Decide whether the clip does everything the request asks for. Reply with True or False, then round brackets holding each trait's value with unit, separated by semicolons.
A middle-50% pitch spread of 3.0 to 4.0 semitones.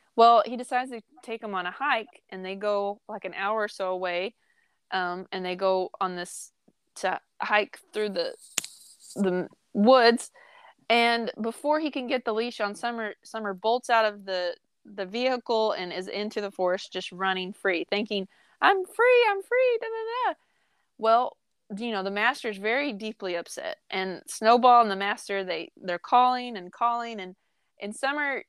False (4.4 semitones)